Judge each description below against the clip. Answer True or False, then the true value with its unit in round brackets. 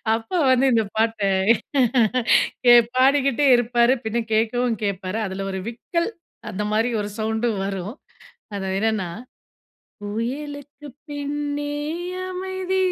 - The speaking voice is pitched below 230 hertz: False (235 Hz)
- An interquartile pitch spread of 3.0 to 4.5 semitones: False (4.9 semitones)